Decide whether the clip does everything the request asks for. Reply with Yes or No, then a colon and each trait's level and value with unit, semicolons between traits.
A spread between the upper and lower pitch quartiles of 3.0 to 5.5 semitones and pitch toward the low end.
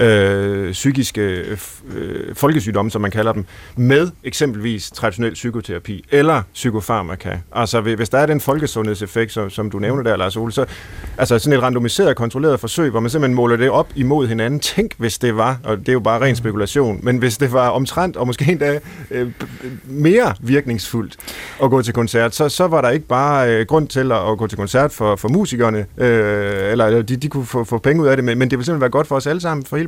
Yes: average, 4.1 semitones; low, 120 Hz